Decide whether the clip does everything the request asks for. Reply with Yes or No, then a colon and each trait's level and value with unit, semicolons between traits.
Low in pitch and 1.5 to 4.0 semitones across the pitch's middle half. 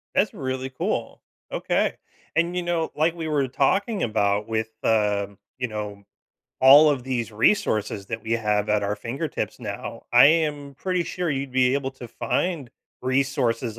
No: low, 130 Hz; average, 5.2 semitones